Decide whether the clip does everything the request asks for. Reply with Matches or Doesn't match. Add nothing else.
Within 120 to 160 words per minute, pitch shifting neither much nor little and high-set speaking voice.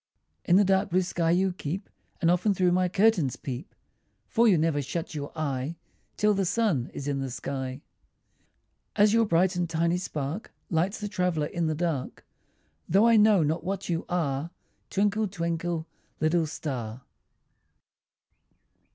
Doesn't match